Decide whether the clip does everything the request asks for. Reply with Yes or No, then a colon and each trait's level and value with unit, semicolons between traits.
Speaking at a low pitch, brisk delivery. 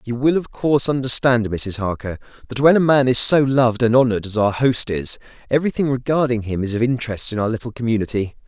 Yes: low, 120 Hz; fast, 210 wpm